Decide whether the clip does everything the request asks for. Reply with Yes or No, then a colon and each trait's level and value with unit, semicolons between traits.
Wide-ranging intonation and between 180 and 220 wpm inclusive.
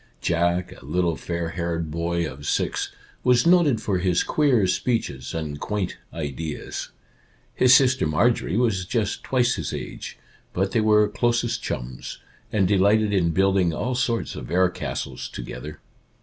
No: wide, 5.8 semitones; average, 150 wpm